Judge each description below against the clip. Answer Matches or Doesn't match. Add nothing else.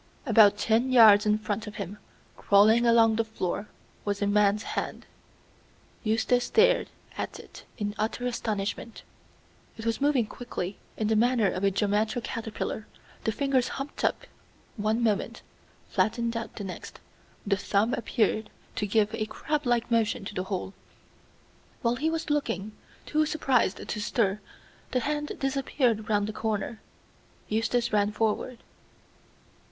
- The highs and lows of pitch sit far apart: Doesn't match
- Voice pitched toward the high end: Matches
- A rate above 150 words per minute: Doesn't match